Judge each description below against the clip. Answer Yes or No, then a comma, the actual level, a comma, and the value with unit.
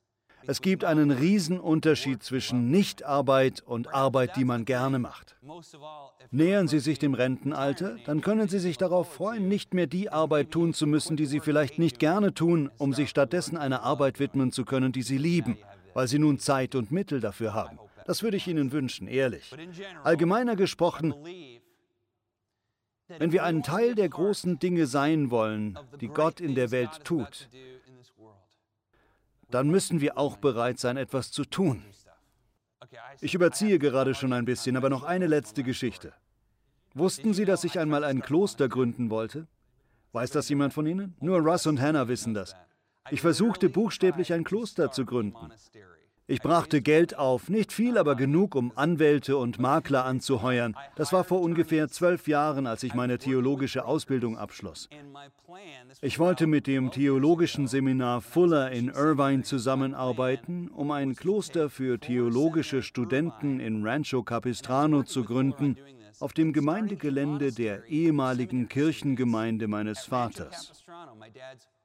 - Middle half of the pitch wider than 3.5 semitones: Yes, average, 4.4 semitones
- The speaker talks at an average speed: Yes, average, 150 wpm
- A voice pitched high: No, medium, 140 Hz